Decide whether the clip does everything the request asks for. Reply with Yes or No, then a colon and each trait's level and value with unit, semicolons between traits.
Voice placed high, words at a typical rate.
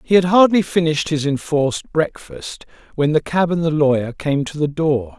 No: medium, 155 Hz; average, 195 wpm